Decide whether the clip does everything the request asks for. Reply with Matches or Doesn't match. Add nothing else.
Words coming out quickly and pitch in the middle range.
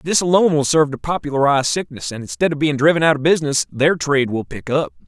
Matches